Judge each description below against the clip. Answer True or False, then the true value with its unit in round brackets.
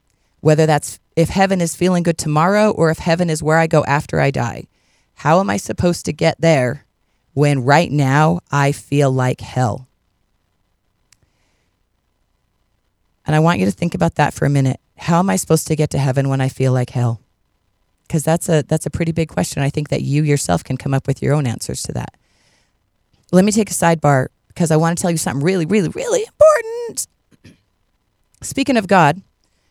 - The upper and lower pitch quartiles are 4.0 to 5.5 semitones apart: True (4.6 semitones)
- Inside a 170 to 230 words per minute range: True (195 wpm)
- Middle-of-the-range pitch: True (150 Hz)